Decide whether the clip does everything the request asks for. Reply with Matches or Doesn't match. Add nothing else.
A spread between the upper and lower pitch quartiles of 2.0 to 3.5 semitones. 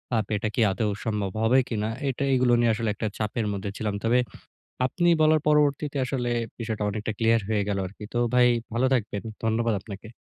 Matches